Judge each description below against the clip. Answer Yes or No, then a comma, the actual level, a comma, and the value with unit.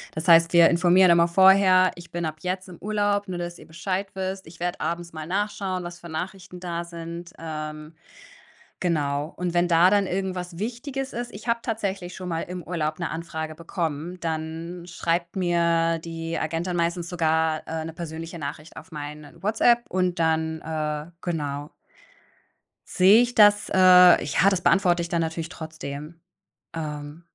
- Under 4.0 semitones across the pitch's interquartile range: Yes, narrow, 2.4 semitones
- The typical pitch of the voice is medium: Yes, medium, 170 Hz